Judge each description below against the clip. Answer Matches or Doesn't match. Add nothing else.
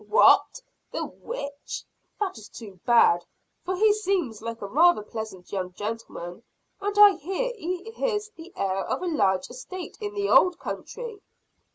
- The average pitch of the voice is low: Doesn't match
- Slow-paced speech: Doesn't match